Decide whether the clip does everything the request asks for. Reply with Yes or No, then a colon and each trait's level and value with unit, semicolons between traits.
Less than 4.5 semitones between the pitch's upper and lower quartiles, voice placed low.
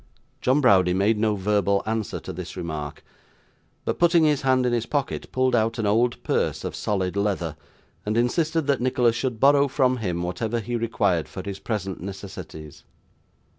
No: average, 4.8 semitones; low, 110 Hz